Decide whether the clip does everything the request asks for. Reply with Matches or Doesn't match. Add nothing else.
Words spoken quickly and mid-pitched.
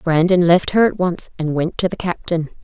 Matches